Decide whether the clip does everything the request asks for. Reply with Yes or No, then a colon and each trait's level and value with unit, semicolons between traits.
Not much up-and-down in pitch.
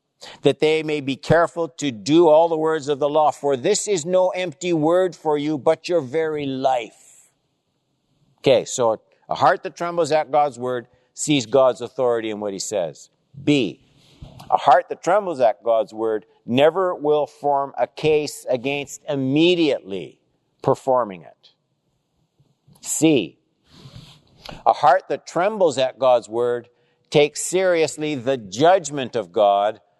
No: average, 3.5 semitones